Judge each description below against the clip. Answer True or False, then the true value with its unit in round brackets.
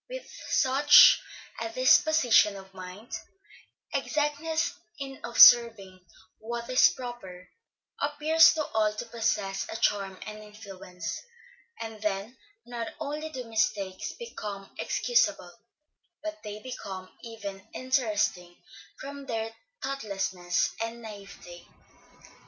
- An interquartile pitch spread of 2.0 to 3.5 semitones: False (5.3 semitones)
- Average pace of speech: False (105 wpm)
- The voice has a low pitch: False (225 Hz)